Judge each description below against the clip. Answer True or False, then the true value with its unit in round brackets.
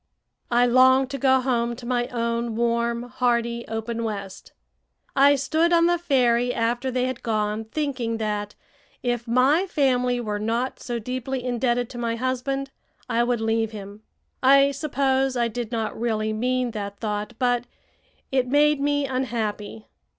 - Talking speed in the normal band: True (155 wpm)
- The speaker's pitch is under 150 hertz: False (245 Hz)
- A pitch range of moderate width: False (2.3 semitones)